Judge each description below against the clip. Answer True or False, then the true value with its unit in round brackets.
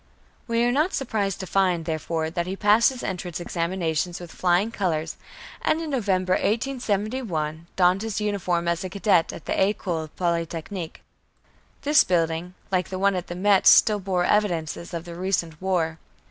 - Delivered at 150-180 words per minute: True (160 wpm)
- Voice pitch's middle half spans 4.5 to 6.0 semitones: False (3.4 semitones)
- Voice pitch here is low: False (185 Hz)